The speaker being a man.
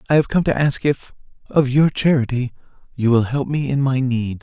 Yes: male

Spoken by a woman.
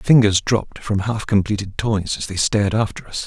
No: male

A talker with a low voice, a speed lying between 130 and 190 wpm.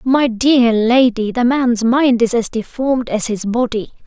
No: high, 235 Hz; average, 175 wpm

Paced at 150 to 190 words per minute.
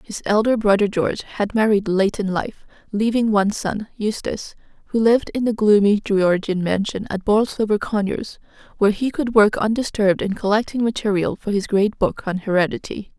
Yes: average, 170 wpm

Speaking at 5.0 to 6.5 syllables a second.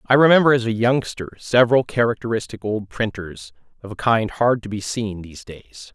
Yes: 5.2 syllables/s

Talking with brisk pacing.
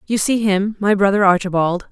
No: average, 155 wpm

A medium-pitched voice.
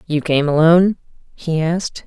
Yes: medium, 165 Hz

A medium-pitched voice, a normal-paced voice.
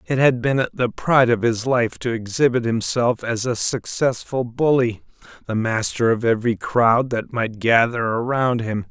No: low, 120 Hz; average, 160 wpm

